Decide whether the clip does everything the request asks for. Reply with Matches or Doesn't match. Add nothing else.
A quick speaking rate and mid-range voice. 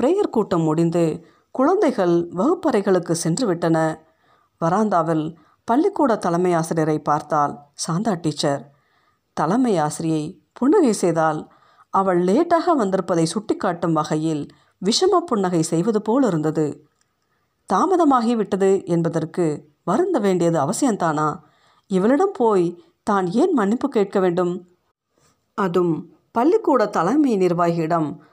Doesn't match